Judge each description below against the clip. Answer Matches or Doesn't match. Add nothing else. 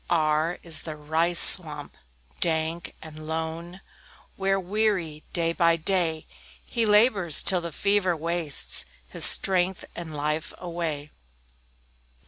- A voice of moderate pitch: Matches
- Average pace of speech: Doesn't match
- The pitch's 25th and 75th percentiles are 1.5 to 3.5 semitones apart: Matches